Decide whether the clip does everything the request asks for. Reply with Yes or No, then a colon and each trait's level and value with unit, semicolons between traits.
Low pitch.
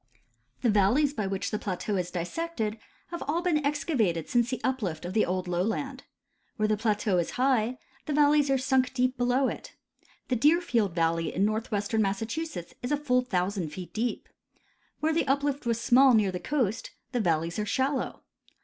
No: high, 230 Hz